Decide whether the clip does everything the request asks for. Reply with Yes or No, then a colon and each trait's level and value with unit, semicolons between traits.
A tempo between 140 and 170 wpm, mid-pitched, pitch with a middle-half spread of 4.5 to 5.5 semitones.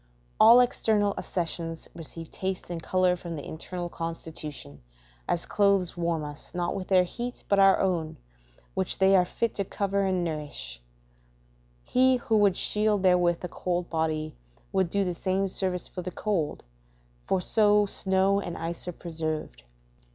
No: average, 160 wpm; medium, 180 Hz; average, 3.0 semitones